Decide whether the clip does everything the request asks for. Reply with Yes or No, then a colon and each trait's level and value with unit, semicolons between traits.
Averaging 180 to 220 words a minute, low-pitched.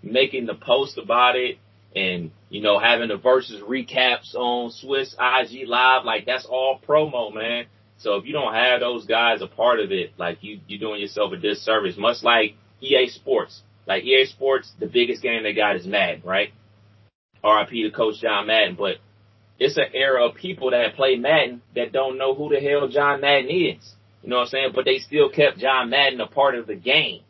Yes: fast, 205 wpm; low, 125 Hz